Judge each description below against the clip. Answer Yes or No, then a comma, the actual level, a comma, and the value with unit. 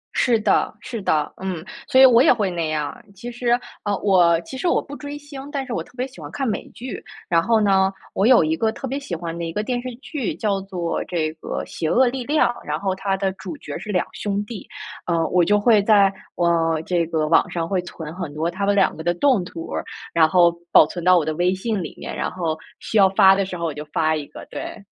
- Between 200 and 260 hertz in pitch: No, high, 190 Hz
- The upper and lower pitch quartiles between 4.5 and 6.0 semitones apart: Yes, wide, 5.5 semitones